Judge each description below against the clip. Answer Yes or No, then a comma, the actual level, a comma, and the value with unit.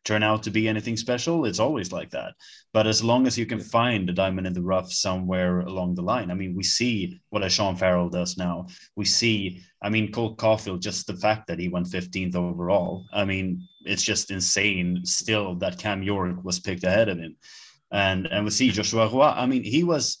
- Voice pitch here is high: No, low, 100 Hz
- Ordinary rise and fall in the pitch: Yes, average, 3.3 semitones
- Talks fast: Yes, fast, 215 wpm